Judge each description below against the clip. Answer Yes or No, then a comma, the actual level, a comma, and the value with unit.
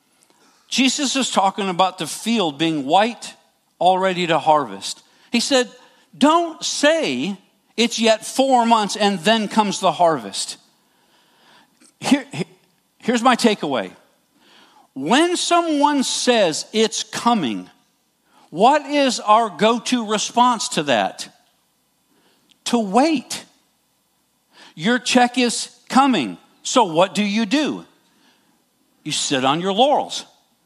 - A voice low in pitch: No, high, 235 Hz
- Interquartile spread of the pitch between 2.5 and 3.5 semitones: No, average, 4.5 semitones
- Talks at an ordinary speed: No, slow, 110 wpm